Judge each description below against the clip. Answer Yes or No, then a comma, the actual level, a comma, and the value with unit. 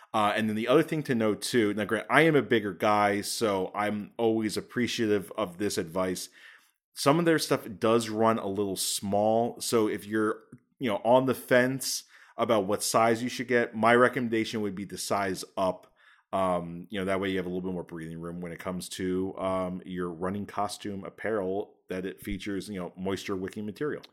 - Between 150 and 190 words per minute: No, fast, 205 wpm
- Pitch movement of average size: Yes, average, 3.4 semitones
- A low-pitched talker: Yes, low, 105 Hz